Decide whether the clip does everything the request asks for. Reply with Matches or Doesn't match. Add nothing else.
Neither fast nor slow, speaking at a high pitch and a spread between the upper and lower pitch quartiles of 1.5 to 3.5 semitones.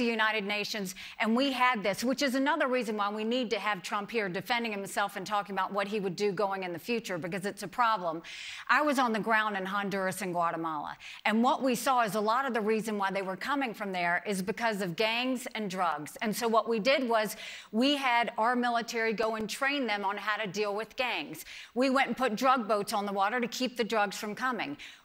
Doesn't match